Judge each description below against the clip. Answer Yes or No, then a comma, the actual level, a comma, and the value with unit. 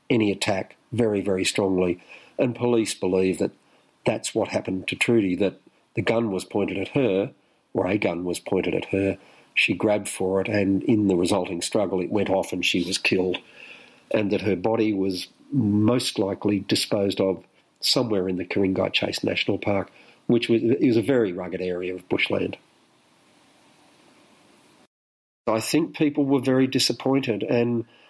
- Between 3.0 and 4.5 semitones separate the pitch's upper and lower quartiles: Yes, average, 3.7 semitones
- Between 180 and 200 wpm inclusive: No, average, 165 wpm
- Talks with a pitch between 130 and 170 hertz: No, low, 100 Hz